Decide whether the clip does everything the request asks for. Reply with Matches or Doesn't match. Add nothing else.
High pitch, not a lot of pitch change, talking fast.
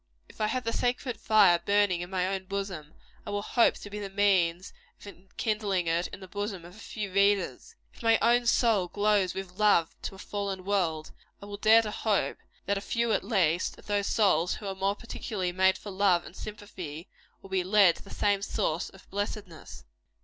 Matches